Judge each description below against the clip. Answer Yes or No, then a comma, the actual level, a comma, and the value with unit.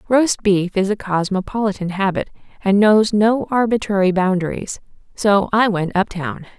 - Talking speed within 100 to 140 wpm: Yes, slow, 135 wpm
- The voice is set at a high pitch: Yes, high, 200 Hz